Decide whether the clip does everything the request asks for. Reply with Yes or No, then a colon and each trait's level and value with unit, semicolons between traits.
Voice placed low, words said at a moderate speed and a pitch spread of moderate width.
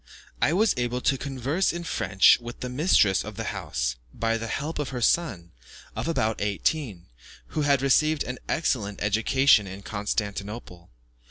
No: low, 120 Hz; average, 160 wpm; wide, 5.8 semitones